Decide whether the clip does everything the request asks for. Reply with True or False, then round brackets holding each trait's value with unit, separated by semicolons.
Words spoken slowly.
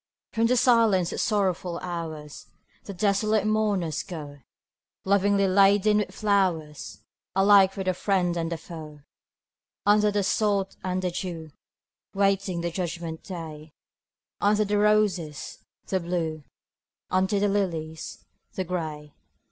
True (125 wpm)